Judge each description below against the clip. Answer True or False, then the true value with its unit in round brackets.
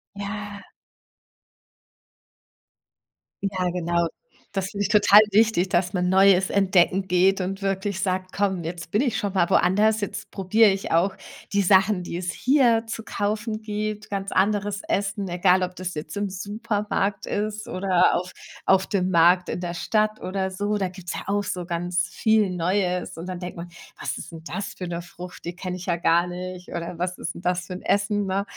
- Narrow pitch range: True (2.3 semitones)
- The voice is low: False (190 Hz)